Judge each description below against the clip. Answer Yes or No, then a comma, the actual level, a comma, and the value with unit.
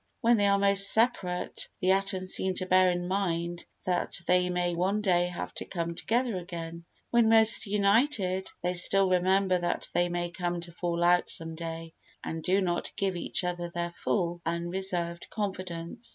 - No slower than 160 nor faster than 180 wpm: Yes, average, 175 wpm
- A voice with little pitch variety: Yes, narrow, 2.2 semitones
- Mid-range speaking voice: Yes, medium, 180 Hz